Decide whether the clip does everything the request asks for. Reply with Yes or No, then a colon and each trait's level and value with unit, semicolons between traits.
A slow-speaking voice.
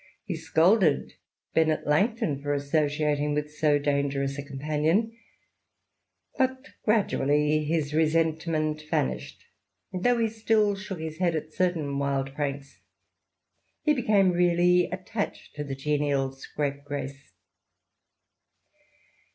Yes: slow, 110 wpm